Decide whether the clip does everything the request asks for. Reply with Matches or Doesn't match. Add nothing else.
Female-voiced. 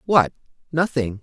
Doesn't match